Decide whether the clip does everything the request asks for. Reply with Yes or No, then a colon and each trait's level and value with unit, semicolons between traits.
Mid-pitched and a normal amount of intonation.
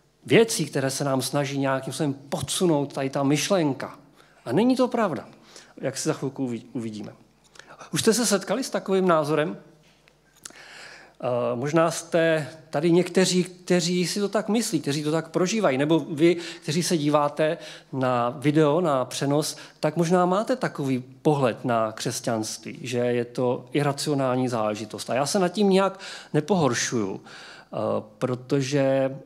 Yes: medium, 150 Hz; average, 4.9 semitones